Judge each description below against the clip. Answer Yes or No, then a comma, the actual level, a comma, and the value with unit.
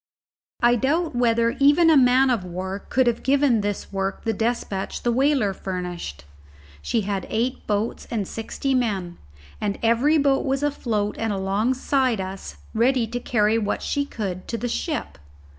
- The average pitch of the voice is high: Yes, high, 230 Hz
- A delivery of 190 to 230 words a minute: No, average, 160 wpm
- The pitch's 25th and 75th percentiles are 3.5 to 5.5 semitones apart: Yes, average, 4.6 semitones